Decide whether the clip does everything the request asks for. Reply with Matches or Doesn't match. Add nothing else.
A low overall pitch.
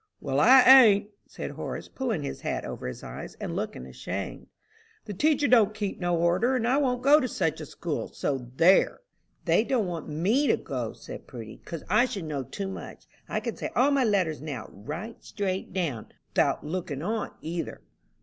Doesn't match